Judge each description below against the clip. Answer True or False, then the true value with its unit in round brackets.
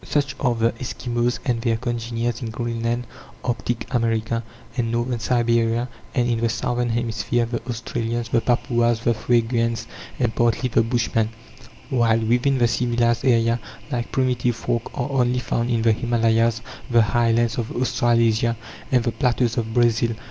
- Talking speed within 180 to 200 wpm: False (155 wpm)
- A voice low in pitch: True (120 Hz)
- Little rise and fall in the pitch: True (1.0 semitones)